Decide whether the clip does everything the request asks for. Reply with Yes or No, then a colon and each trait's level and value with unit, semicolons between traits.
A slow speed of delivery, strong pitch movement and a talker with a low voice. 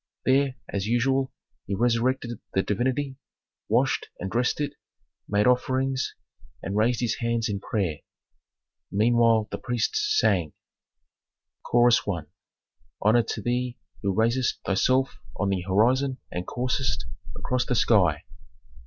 No: slow, 125 wpm; average, 4.1 semitones; low, 120 Hz